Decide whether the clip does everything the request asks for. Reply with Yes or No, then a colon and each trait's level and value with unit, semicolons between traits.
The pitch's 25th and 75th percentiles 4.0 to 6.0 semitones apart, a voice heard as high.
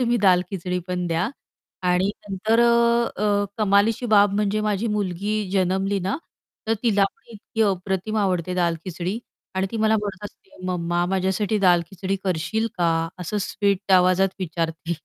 No: average, 2.7 semitones; high, 195 Hz